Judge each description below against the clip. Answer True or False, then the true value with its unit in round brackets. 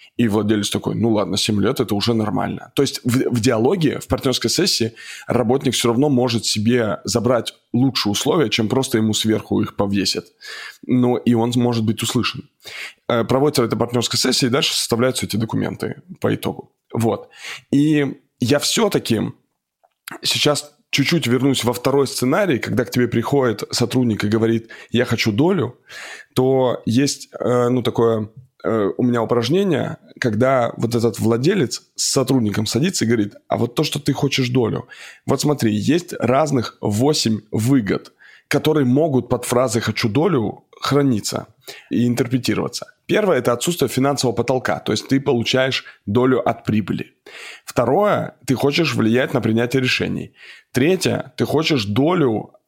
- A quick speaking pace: False (150 wpm)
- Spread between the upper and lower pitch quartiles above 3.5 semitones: False (3.1 semitones)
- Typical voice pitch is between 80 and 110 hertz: False (125 Hz)